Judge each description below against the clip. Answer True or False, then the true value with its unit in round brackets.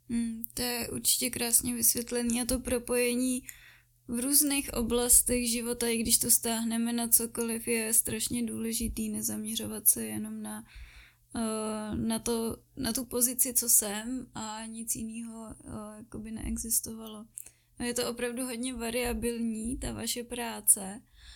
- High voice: True (230 Hz)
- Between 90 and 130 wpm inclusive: True (125 wpm)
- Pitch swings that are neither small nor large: False (1.6 semitones)